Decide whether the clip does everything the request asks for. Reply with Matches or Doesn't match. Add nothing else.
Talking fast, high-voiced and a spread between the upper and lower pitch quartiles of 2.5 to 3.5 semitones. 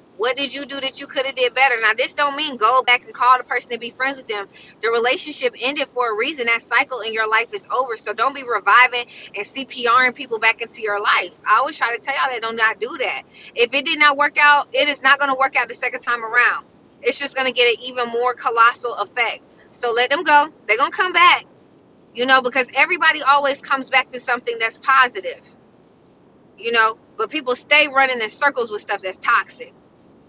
Matches